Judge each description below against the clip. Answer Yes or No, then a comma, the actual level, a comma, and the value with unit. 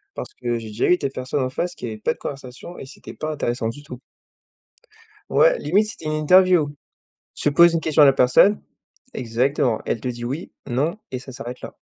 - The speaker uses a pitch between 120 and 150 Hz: Yes, medium, 140 Hz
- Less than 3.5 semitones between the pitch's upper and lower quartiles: No, average, 4.7 semitones